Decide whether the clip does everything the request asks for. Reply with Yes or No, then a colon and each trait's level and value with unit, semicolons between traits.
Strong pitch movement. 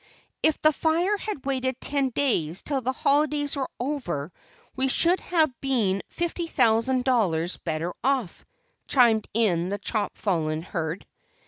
Yes: wide, 7.2 semitones